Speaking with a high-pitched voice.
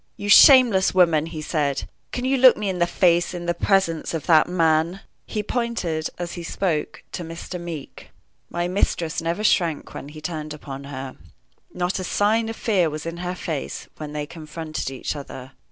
No: medium, 170 Hz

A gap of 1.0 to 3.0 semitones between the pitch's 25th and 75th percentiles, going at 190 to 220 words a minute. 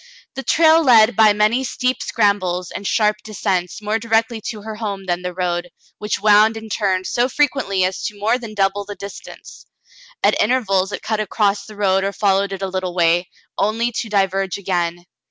Yes: average, 2.7 semitones; average, 195 wpm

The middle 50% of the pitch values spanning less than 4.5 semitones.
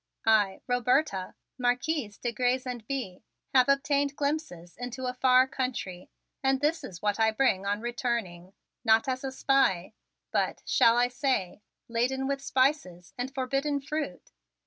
Yes: average, 3.9 semitones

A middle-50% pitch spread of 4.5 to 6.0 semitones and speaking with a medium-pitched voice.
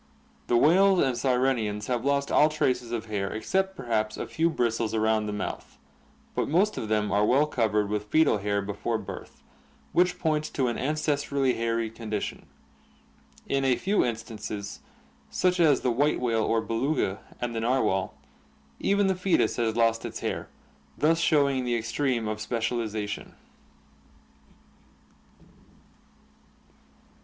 No: average, 5.1 semitones; low, 120 Hz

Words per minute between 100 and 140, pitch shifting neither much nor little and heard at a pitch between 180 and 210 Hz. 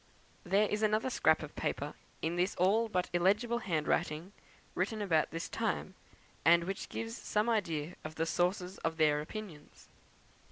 No: average, 155 wpm; average, 4.5 semitones; medium, 185 Hz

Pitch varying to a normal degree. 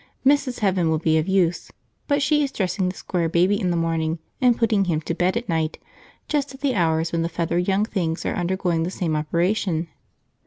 Yes: average, 4.1 semitones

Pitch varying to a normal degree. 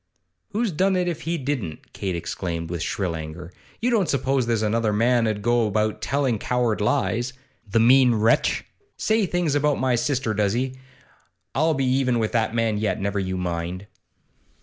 Yes: average, 4.9 semitones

